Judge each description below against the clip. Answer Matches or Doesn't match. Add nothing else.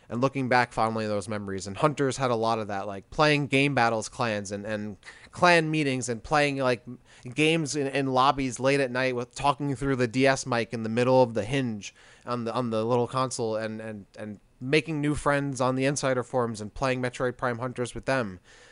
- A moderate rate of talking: Doesn't match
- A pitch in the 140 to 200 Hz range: Doesn't match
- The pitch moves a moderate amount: Matches